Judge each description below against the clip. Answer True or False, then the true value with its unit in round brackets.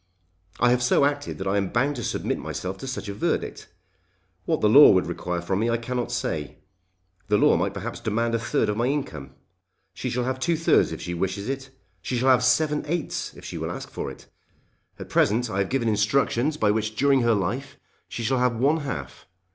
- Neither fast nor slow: False (220 wpm)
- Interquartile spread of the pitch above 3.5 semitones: True (4.4 semitones)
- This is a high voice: False (120 Hz)